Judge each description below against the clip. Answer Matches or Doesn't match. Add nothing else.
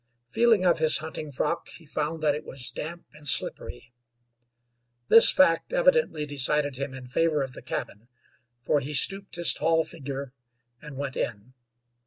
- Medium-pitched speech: Matches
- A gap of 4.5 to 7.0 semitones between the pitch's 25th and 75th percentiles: Doesn't match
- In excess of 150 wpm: Matches